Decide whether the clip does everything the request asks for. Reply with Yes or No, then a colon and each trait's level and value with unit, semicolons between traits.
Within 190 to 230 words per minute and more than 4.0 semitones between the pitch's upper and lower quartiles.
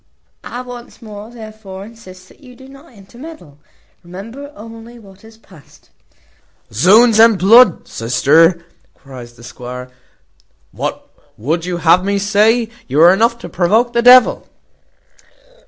No: average, 140 wpm; average, 5.3 semitones